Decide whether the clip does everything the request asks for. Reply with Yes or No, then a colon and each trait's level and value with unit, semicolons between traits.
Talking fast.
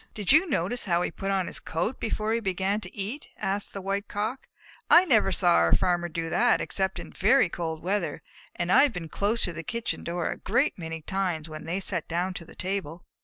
Yes: fast, 225 wpm